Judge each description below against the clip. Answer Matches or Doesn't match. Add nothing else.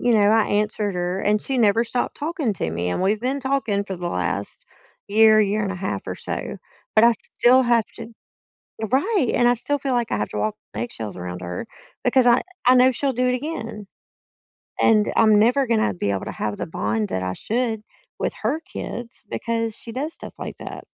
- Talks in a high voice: Matches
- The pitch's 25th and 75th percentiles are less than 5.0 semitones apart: Doesn't match